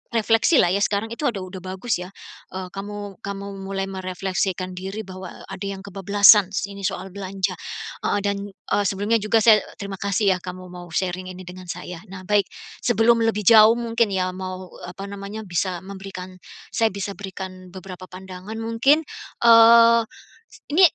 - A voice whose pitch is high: Yes, high, 195 Hz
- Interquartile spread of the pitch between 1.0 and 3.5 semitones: Yes, narrow, 2.4 semitones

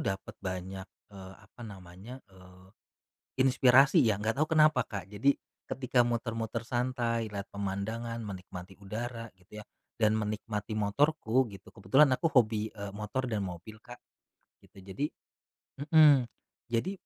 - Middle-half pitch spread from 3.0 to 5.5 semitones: Yes, average, 3.8 semitones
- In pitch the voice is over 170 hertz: No, low, 110 Hz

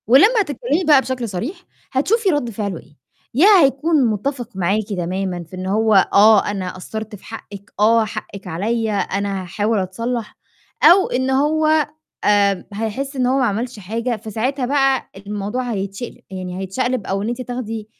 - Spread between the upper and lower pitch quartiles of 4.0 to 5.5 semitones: Yes, average, 4.7 semitones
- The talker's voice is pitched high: Yes, high, 220 Hz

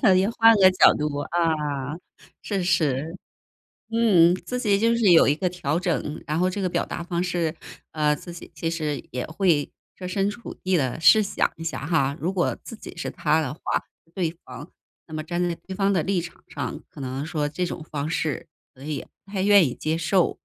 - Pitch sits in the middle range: Yes, medium, 170 Hz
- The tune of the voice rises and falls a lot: No, average, 3.7 semitones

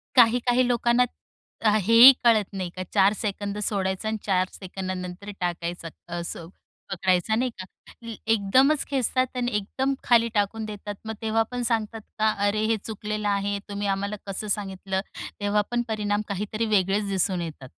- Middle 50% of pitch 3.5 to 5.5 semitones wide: No, average, 2.9 semitones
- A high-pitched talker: Yes, high, 205 Hz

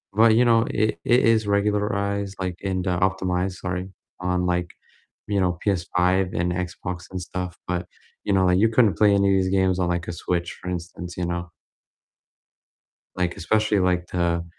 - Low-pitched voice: Yes, very low, 90 Hz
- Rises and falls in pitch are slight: Yes, narrow, 2.2 semitones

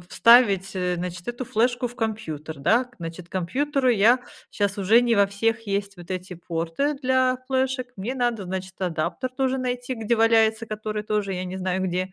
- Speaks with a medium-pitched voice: No, high, 215 Hz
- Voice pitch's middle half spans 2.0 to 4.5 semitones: No, average, 4.9 semitones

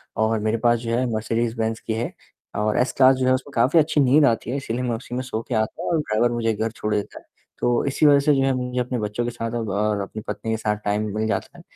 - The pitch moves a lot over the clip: No, average, 2.8 semitones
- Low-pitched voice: Yes, low, 115 Hz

